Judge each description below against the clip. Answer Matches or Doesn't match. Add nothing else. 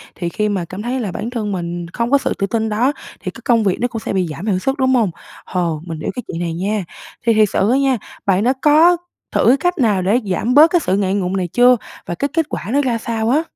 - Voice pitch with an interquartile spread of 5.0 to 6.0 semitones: Matches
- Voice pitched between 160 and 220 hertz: Matches